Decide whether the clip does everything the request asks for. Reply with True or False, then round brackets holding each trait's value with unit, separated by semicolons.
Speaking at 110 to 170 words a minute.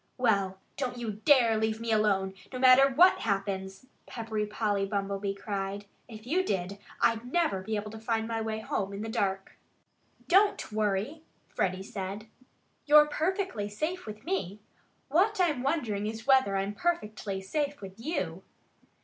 True (160 wpm)